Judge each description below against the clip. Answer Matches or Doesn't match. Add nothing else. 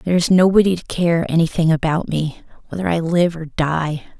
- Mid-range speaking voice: Matches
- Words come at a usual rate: Matches